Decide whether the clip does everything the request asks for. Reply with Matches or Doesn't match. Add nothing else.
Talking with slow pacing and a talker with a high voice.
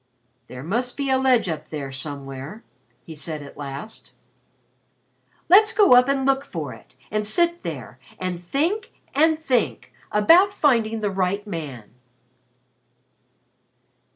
Matches